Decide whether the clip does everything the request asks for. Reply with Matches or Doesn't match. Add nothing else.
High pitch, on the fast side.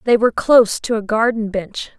Matches